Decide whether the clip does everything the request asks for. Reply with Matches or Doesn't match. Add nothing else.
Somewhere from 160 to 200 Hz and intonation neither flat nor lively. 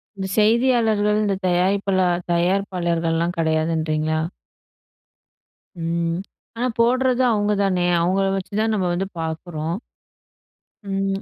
Matches